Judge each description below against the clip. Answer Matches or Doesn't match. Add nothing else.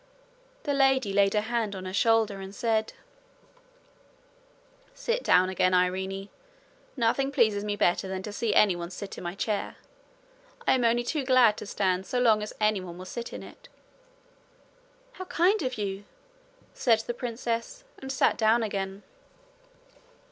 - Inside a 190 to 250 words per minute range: Doesn't match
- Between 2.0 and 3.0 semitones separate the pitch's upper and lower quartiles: Doesn't match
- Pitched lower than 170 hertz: Doesn't match